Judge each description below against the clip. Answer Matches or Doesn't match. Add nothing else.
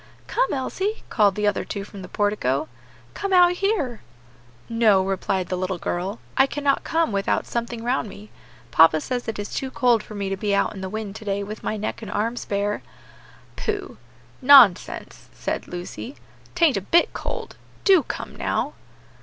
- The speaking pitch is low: Doesn't match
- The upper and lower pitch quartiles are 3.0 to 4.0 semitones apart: Doesn't match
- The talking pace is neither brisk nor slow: Matches